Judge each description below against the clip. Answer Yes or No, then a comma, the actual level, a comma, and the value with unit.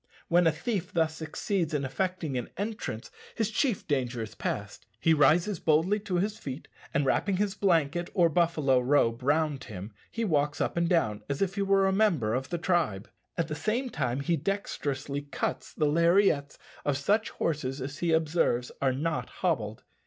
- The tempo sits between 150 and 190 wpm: Yes, average, 180 wpm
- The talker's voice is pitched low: No, medium, 160 Hz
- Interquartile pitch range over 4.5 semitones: Yes, average, 5.1 semitones